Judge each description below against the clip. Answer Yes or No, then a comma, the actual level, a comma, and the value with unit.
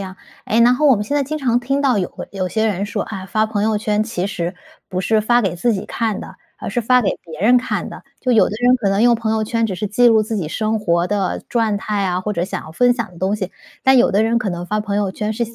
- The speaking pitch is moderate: No, high, 215 Hz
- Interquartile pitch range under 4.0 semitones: Yes, average, 3.4 semitones